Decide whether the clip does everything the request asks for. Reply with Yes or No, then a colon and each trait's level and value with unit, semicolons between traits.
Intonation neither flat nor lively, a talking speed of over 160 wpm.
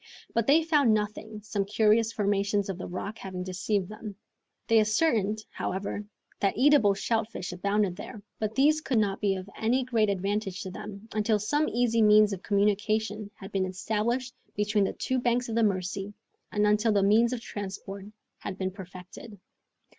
No: narrow, 2.3 semitones; average, 170 wpm